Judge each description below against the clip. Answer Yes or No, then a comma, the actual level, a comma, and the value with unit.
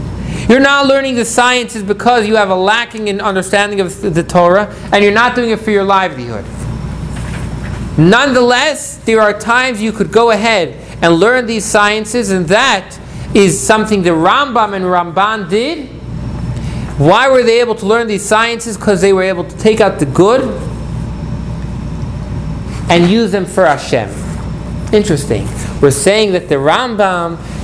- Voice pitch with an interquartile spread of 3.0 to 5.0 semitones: Yes, average, 3.7 semitones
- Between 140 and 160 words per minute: Yes, average, 155 wpm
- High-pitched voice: Yes, high, 210 Hz